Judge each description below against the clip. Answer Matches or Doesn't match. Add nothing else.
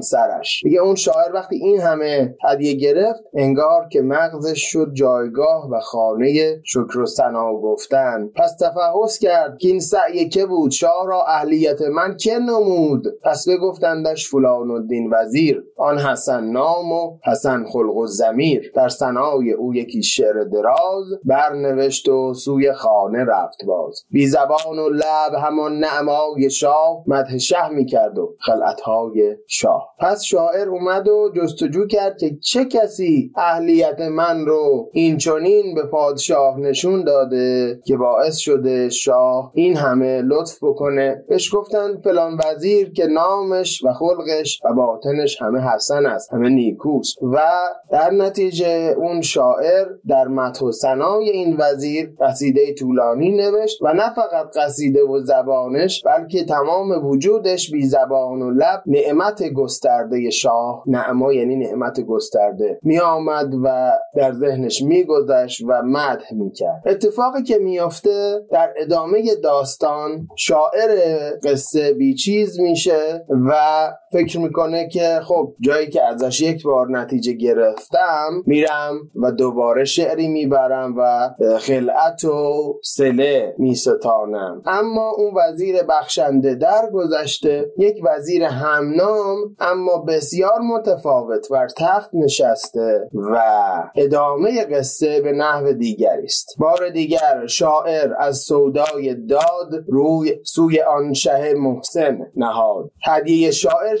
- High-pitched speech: Doesn't match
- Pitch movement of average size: Doesn't match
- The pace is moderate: Matches